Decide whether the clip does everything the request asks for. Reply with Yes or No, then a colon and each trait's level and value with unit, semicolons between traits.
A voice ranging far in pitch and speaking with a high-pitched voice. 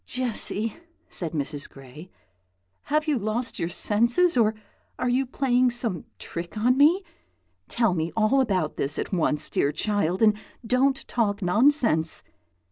Yes: wide, 6.6 semitones; high, 220 Hz